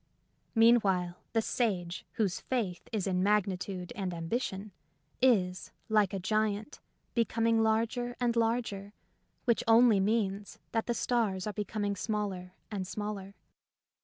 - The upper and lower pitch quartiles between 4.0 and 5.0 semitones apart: No, average, 3.0 semitones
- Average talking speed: No, slow, 130 wpm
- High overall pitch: Yes, high, 210 Hz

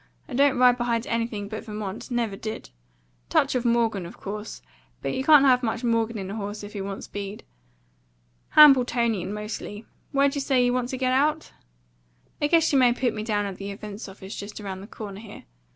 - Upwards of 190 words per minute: Yes, average, 200 wpm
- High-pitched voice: Yes, high, 225 Hz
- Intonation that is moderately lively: Yes, average, 3.5 semitones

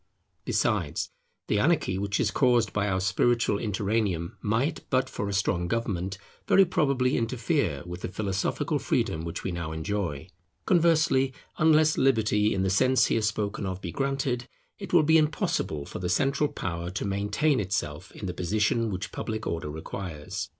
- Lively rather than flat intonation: Yes, wide, 5.9 semitones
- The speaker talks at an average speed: Yes, average, 165 wpm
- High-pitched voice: No, low, 105 Hz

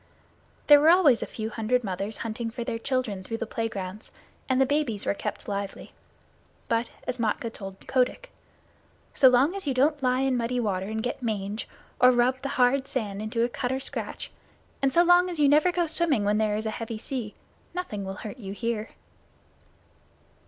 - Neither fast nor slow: Yes, average, 195 wpm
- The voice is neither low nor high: No, high, 240 Hz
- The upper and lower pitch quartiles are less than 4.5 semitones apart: Yes, average, 3.8 semitones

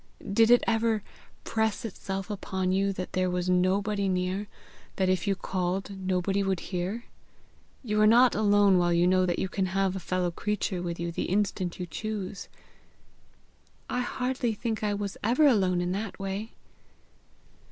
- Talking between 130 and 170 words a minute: Yes, average, 165 wpm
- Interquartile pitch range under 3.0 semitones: Yes, narrow, 2.5 semitones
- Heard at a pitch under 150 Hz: No, high, 195 Hz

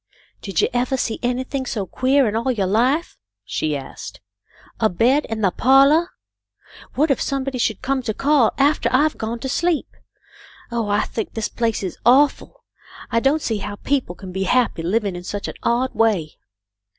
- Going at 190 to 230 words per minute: Yes, average, 195 wpm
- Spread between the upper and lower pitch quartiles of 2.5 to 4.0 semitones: No, average, 4.6 semitones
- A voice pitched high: Yes, high, 240 Hz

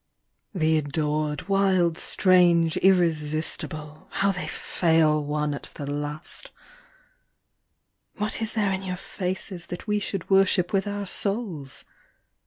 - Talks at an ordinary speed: No, slow, 120 wpm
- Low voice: No, medium, 175 Hz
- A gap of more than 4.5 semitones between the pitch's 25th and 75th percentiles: No, average, 4.1 semitones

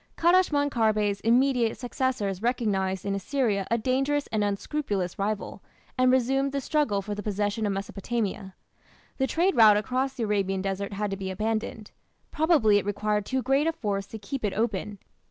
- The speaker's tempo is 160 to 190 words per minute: Yes, average, 170 wpm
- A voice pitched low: No, high, 215 Hz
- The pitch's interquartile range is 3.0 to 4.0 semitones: No, average, 4.6 semitones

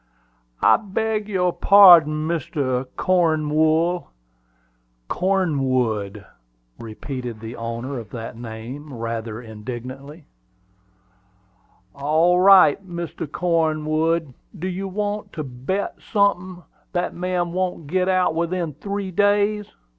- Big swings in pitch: Yes, wide, 6.1 semitones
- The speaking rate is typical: No, slow, 100 wpm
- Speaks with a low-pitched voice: No, medium, 165 Hz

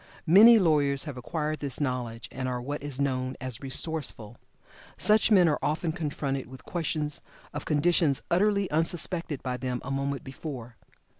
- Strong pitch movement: No, average, 4.1 semitones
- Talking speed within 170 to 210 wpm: No, average, 155 wpm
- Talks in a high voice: No, medium, 145 Hz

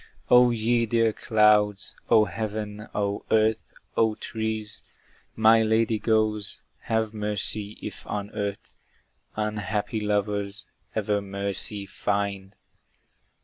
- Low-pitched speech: Yes, low, 105 Hz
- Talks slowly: Yes, slow, 105 wpm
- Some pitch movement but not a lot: No, narrow, 1.4 semitones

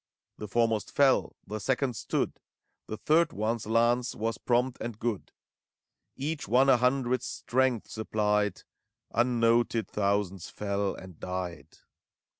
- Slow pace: Yes, slow, 120 wpm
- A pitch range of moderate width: Yes, average, 3.2 semitones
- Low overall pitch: Yes, low, 115 Hz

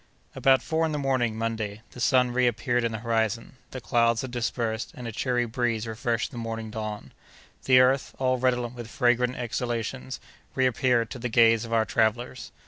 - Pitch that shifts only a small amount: Yes, narrow, 1.9 semitones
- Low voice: Yes, low, 120 Hz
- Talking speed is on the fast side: No, average, 180 wpm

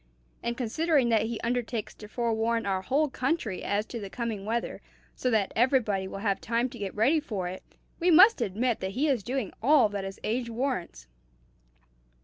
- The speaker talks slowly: No, average, 185 wpm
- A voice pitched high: Yes, high, 230 Hz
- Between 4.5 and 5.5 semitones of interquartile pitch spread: No, average, 3.8 semitones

